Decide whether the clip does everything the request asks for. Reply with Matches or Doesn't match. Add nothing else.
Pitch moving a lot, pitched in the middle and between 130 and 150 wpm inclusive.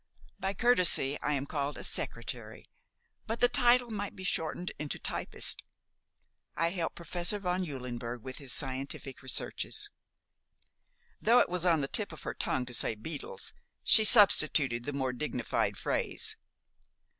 Matches